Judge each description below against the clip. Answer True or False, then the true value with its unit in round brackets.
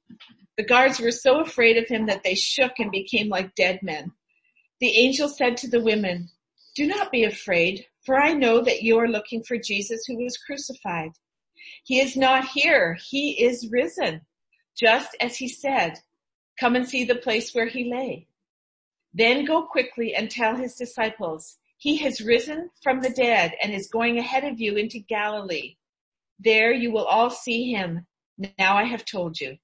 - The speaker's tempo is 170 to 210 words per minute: True (180 wpm)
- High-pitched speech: True (235 Hz)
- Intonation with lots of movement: False (3.6 semitones)